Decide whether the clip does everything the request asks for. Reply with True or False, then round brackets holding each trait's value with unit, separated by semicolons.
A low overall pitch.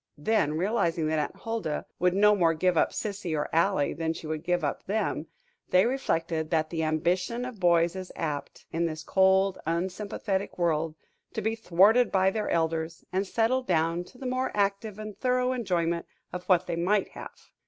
False (180 Hz)